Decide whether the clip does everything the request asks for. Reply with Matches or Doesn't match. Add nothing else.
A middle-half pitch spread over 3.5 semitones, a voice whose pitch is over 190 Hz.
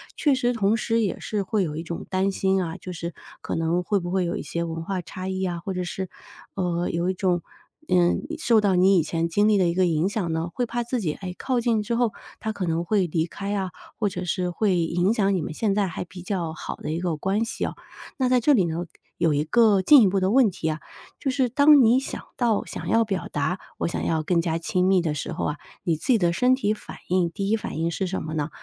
Doesn't match